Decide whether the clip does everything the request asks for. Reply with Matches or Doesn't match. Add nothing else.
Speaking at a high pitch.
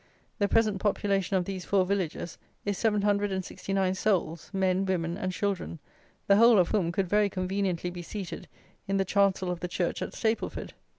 Matches